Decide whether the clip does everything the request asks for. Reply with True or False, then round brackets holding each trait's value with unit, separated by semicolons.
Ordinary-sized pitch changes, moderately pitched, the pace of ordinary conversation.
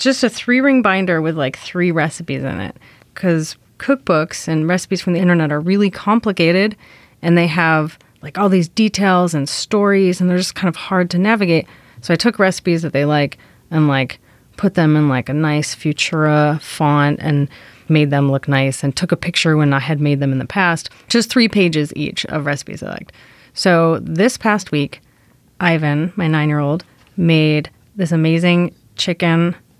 True (3.9 semitones; 165 Hz; 185 wpm)